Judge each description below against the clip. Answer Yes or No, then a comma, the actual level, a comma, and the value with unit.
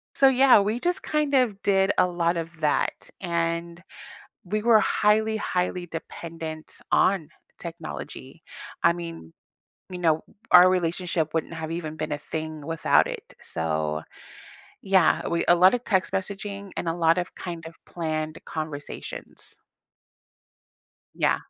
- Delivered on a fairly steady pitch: No, average, 3.2 semitones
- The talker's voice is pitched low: No, medium, 170 Hz